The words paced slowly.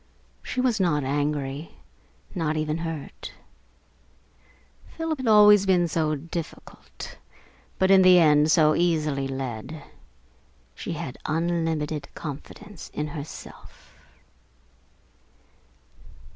Yes: slow, 95 wpm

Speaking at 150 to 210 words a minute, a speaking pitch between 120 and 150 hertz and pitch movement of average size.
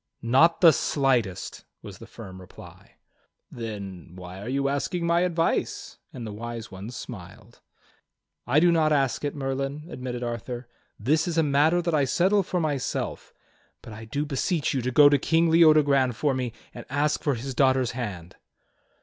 Yes: average, 170 wpm; low, 135 Hz; average, 4.6 semitones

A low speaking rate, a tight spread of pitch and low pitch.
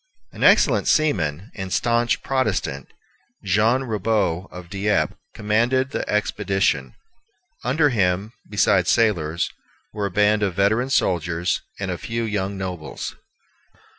No: slow, 120 wpm; average, 3.9 semitones; low, 105 Hz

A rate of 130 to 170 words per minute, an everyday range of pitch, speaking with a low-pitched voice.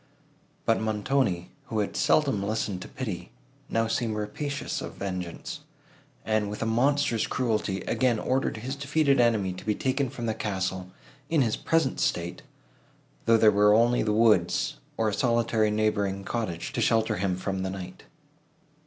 Yes: average, 160 wpm; average, 3.4 semitones; low, 110 Hz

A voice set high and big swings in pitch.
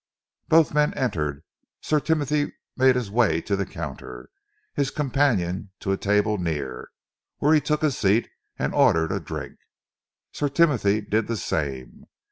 No: low, 105 Hz; wide, 8.7 semitones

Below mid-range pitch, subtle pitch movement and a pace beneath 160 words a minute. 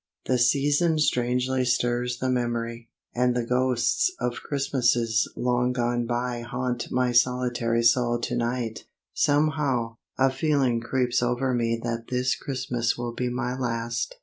Yes: low, 125 Hz; narrow, 1.3 semitones; average, 140 wpm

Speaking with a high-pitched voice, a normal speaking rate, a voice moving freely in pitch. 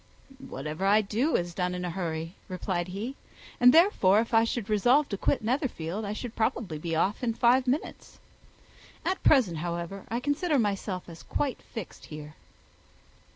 Yes: high, 205 Hz; average, 165 wpm; wide, 5.9 semitones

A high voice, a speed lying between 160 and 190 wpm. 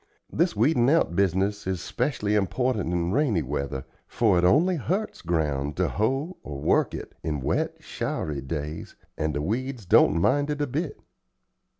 No: low, 100 Hz; average, 165 wpm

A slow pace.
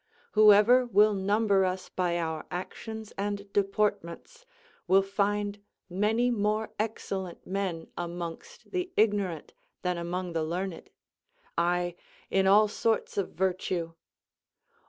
Yes: slow, 115 wpm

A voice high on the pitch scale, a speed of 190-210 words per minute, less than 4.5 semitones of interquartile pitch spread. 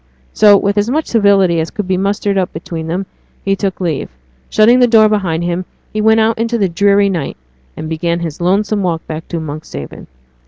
Yes: high, 195 Hz; average, 200 wpm; average, 3.8 semitones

